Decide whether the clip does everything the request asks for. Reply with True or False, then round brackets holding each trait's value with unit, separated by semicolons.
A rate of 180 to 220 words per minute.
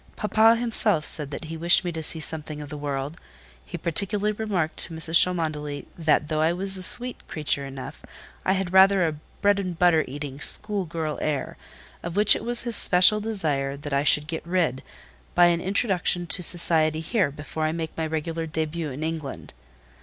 True (190 wpm)